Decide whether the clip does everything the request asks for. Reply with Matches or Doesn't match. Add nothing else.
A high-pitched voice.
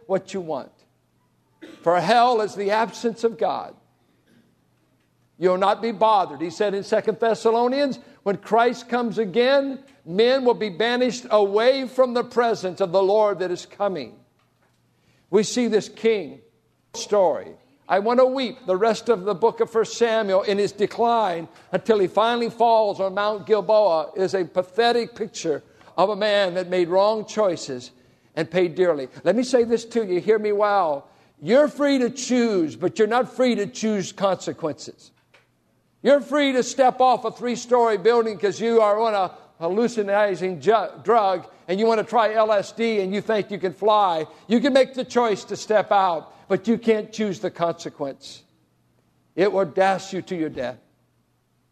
Matches